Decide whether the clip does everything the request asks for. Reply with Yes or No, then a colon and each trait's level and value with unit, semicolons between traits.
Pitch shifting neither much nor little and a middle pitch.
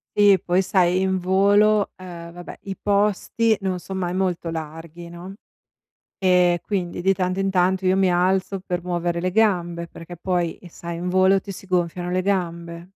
No: narrow, 1.7 semitones; medium, 180 Hz